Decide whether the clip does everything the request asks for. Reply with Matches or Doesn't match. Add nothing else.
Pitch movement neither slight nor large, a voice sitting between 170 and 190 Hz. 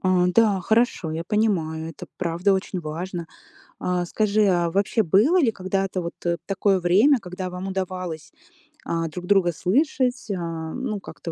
Matches